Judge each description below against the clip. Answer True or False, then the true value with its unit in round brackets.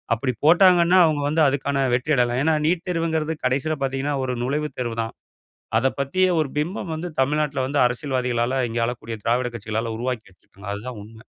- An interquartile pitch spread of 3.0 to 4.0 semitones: False (4.4 semitones)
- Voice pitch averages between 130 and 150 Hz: True (135 Hz)